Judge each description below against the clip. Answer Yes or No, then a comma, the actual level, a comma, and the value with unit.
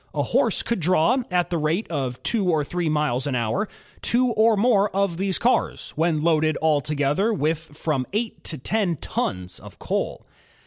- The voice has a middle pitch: Yes, medium, 165 Hz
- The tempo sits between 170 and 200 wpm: Yes, average, 175 wpm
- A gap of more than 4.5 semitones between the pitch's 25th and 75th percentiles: Yes, average, 5.1 semitones